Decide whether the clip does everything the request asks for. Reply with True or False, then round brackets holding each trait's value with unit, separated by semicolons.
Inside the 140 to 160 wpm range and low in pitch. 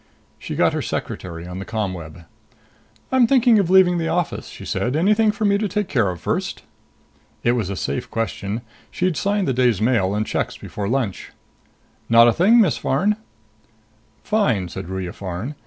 False (175 wpm; 125 Hz)